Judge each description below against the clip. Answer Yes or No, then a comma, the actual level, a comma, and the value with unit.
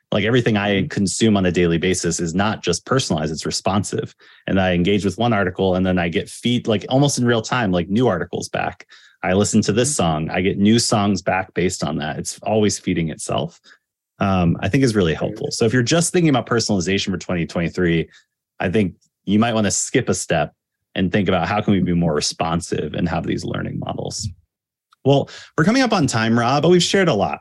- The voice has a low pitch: Yes, low, 105 Hz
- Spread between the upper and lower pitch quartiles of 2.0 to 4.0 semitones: No, average, 4.6 semitones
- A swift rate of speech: Yes, fast, 220 wpm